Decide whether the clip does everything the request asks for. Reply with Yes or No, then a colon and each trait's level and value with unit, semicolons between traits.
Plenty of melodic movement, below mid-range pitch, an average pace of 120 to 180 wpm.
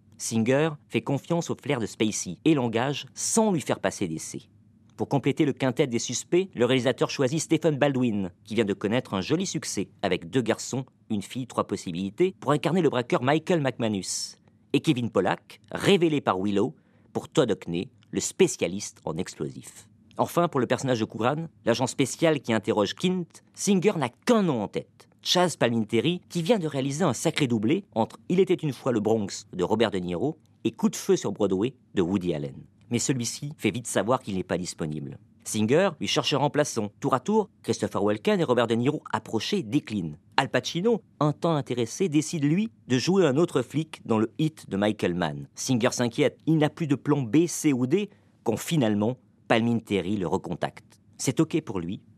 No: wide, 6.3 semitones; low, 130 Hz; average, 190 wpm